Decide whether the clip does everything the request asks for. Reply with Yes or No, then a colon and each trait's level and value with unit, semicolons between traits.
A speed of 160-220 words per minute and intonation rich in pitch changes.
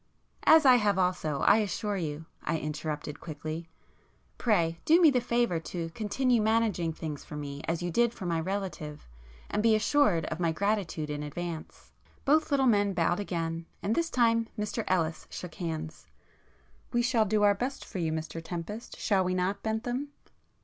Yes: average, 175 wpm; wide, 5.7 semitones